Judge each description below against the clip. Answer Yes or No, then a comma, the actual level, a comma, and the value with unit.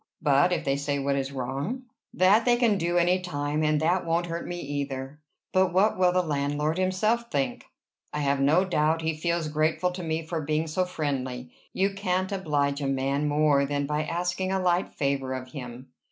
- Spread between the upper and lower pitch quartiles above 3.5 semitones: Yes, average, 4.3 semitones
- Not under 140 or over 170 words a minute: No, average, 195 wpm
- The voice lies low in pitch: No, medium, 155 Hz